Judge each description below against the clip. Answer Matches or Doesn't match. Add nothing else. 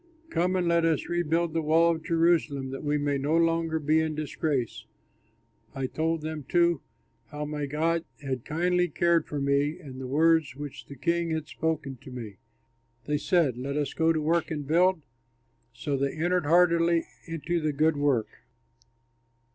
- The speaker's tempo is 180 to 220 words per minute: Doesn't match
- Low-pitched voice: Doesn't match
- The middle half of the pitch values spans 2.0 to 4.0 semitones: Matches